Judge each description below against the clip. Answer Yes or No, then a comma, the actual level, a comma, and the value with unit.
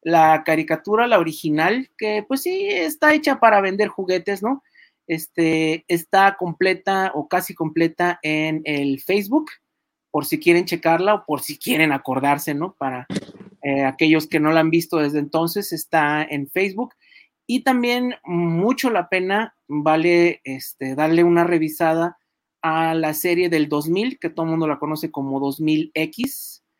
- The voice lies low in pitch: No, medium, 170 Hz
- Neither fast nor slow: Yes, average, 150 wpm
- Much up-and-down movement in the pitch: No, average, 4.8 semitones